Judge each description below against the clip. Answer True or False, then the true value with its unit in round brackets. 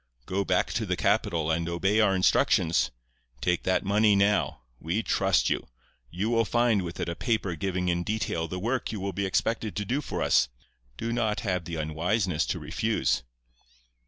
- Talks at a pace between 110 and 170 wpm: False (185 wpm)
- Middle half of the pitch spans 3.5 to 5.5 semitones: True (4.0 semitones)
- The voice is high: False (95 Hz)